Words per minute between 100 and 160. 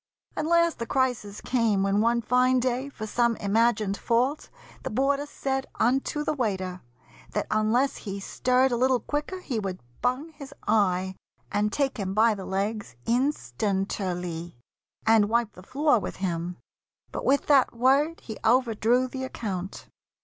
Yes: average, 155 wpm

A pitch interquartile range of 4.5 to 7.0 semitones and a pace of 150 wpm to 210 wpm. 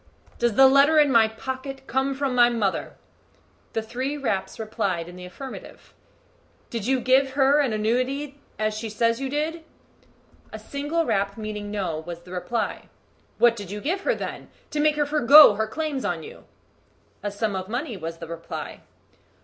Yes: average, 5.0 semitones; average, 175 wpm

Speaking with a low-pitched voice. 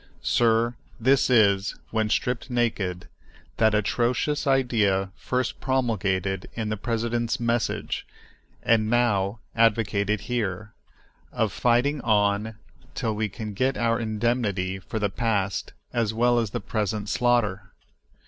Yes: low, 110 Hz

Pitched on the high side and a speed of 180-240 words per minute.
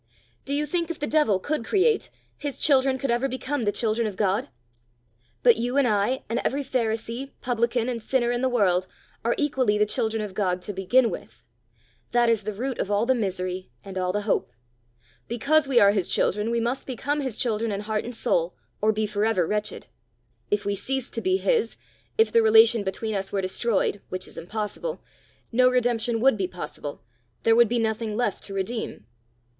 Yes: high, 230 Hz; average, 200 wpm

